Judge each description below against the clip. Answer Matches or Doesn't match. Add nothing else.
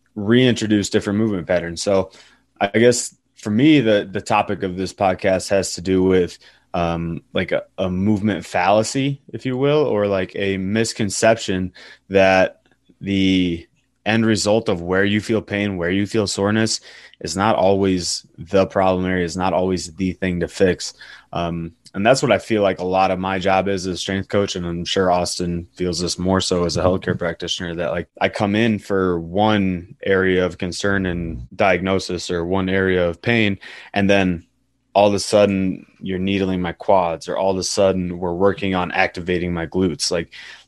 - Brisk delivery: Doesn't match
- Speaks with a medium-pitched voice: Doesn't match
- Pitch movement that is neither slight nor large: Doesn't match